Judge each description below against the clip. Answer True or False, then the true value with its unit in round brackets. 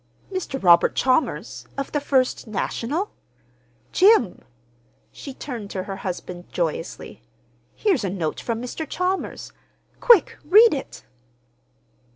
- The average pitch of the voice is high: True (260 Hz)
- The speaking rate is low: True (110 wpm)